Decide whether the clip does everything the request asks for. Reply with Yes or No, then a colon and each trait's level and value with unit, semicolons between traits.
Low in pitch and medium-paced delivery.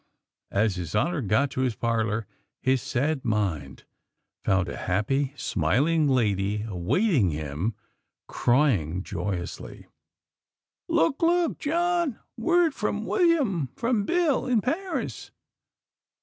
No: low, 130 Hz; slow, 110 wpm